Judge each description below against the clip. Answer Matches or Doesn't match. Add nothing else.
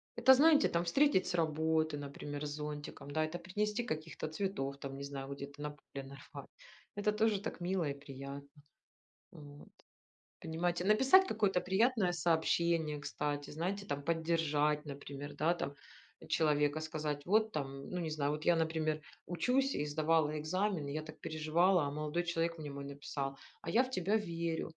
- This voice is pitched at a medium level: Matches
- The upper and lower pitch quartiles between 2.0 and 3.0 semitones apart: Doesn't match